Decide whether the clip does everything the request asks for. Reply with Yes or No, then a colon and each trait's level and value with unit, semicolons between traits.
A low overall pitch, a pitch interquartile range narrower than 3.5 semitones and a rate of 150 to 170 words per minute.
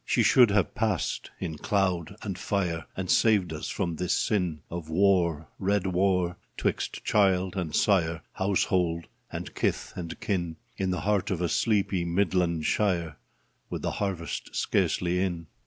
Yes: very low, 90 Hz; narrow, 2.6 semitones; average, 160 wpm